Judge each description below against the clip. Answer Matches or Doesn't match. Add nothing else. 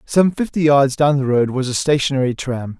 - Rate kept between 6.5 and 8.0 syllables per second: Doesn't match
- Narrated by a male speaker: Matches